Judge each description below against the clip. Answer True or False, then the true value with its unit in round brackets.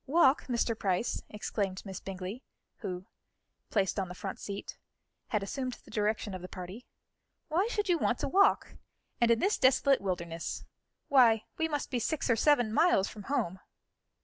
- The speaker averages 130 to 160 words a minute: False (170 wpm)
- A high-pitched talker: True (225 Hz)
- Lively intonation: True (6.1 semitones)